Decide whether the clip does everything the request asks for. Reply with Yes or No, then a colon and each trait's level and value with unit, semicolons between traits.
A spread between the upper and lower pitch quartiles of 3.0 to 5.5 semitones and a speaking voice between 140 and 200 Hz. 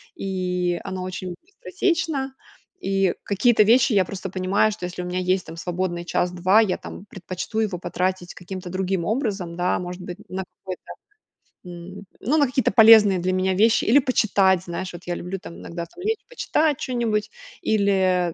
Yes: average, 3.4 semitones; high, 190 Hz